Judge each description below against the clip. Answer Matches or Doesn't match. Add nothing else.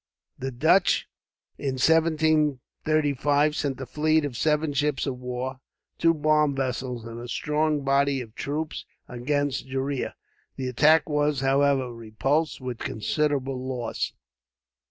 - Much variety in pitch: Doesn't match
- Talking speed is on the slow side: Matches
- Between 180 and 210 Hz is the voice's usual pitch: Doesn't match